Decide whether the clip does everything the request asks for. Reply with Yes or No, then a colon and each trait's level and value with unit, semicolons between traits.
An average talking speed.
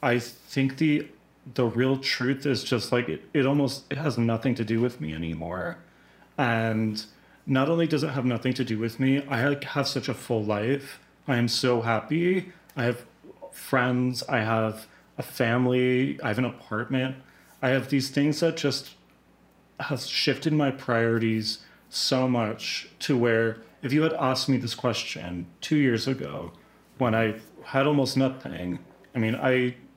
Yes: average, 170 wpm